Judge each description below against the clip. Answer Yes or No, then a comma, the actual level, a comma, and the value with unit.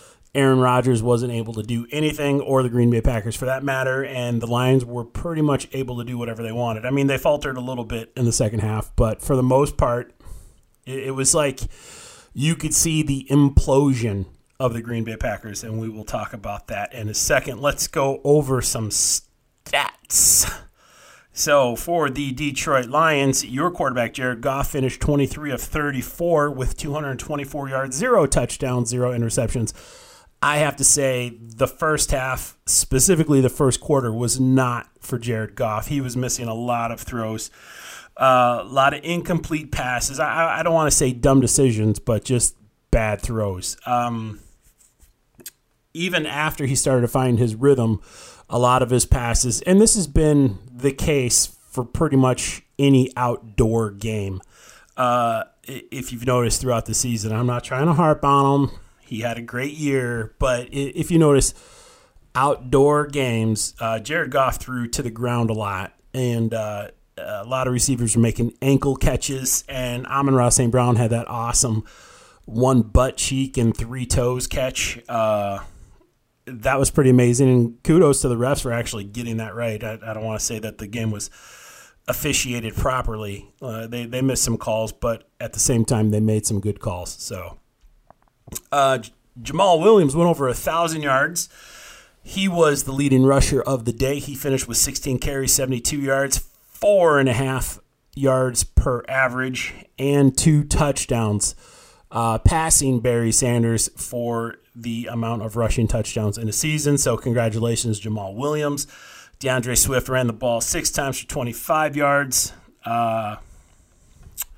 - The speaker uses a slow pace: No, average, 170 wpm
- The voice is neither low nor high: No, low, 125 Hz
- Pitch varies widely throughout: No, average, 3.1 semitones